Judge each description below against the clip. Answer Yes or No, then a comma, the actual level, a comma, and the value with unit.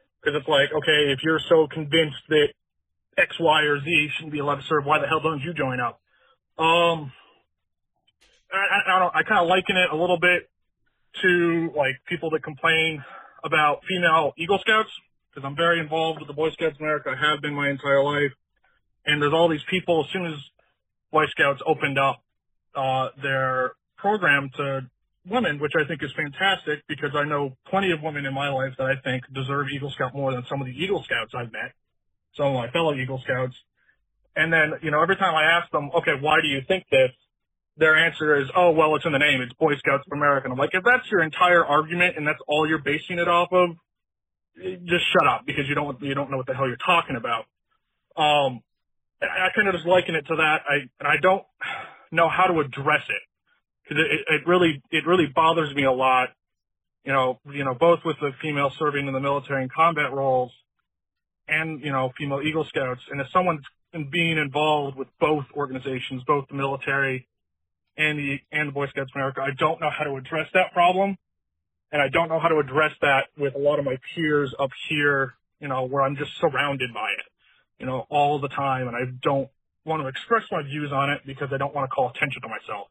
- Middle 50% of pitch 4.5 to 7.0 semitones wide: No, average, 3.0 semitones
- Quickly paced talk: Yes, fast, 215 wpm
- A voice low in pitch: No, medium, 150 Hz